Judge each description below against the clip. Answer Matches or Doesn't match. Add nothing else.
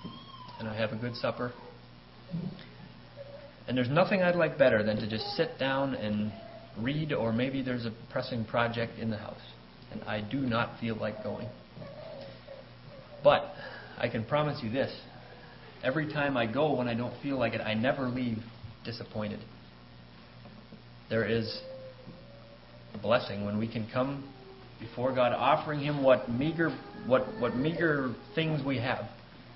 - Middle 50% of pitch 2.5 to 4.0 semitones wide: Matches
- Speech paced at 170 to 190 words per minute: Doesn't match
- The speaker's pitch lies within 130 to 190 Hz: Doesn't match